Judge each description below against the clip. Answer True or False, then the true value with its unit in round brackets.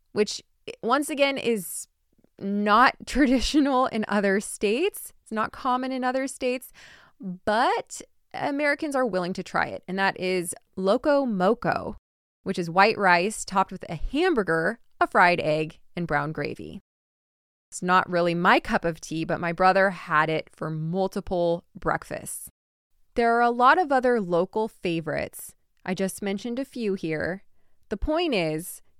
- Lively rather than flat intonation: True (6.3 semitones)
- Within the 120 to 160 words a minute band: True (150 wpm)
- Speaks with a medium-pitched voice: False (195 Hz)